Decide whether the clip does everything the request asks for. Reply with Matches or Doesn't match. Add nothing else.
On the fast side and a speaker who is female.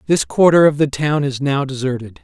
Doesn't match